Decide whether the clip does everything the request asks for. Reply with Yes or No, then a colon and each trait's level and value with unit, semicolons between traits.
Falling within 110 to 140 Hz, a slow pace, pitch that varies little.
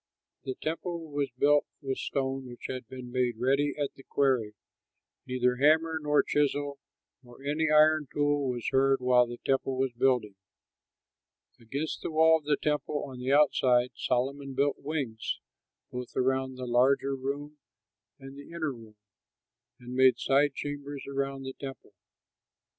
No: low, 135 Hz; average, 150 wpm; narrow, 2.3 semitones